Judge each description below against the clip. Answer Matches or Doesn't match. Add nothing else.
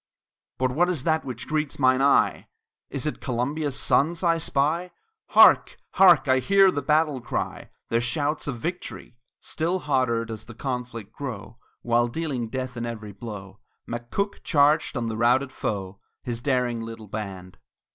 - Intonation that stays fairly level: Doesn't match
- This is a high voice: Doesn't match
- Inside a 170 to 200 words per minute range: Doesn't match